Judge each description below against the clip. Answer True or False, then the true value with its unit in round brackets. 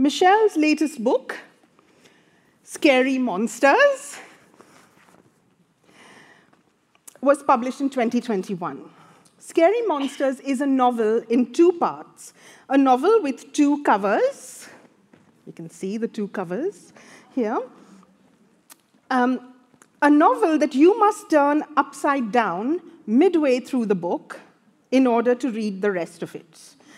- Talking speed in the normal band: False (110 wpm)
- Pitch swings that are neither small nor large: True (4.7 semitones)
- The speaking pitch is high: True (270 Hz)